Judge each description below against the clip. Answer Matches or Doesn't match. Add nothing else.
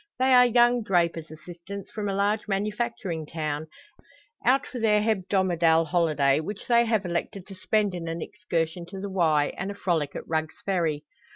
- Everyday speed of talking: Matches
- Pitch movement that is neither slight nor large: Matches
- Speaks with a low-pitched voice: Doesn't match